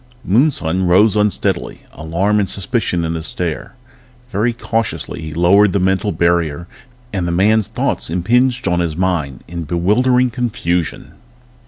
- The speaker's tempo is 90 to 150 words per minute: Yes, average, 140 wpm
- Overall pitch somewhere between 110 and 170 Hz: No, very low, 95 Hz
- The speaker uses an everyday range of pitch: Yes, average, 4.1 semitones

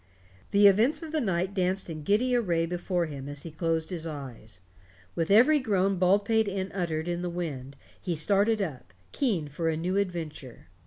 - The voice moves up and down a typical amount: Yes, average, 4.0 semitones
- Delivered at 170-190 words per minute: Yes, average, 180 wpm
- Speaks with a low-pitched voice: No, medium, 175 Hz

